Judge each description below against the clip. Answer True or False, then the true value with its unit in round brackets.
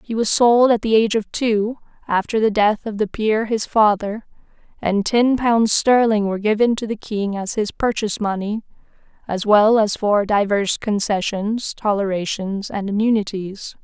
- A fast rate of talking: False (165 wpm)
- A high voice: True (215 Hz)